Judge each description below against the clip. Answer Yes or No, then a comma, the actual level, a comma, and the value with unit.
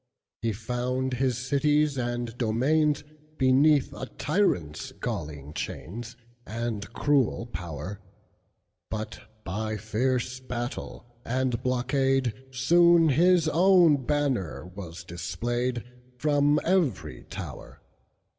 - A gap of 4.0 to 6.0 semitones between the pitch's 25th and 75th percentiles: Yes, average, 4.5 semitones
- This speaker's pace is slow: Yes, slow, 80 wpm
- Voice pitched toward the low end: Yes, low, 125 Hz